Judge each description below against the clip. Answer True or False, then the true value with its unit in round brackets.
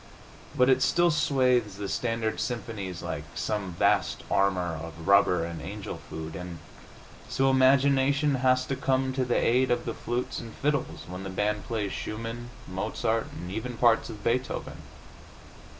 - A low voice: True (115 Hz)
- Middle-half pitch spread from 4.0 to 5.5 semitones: True (5.0 semitones)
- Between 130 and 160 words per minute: True (155 wpm)